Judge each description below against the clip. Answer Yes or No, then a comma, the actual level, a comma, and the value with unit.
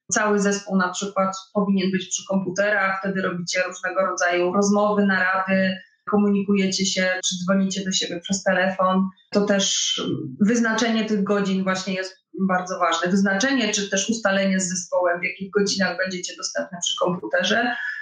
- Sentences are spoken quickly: No, average, 145 wpm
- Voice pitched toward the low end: No, high, 190 Hz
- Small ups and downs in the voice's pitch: Yes, narrow, 1.5 semitones